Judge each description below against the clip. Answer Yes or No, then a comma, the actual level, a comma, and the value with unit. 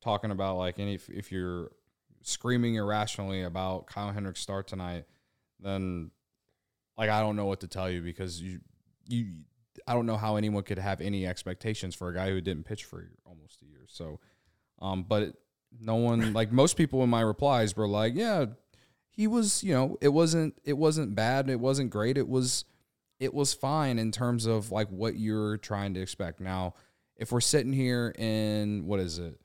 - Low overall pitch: Yes, low, 105 Hz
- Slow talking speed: No, average, 190 wpm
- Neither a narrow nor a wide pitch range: Yes, average, 4.5 semitones